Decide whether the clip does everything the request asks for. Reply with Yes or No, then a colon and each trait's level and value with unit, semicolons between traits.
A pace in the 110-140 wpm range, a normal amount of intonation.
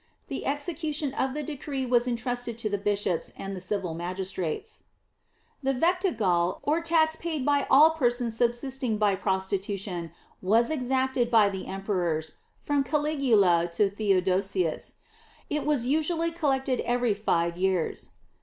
No: slow, 135 wpm; wide, 6.9 semitones